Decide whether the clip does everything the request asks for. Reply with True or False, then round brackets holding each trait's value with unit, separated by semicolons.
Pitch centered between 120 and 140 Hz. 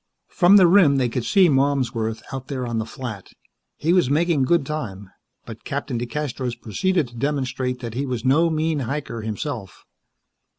True (135 Hz)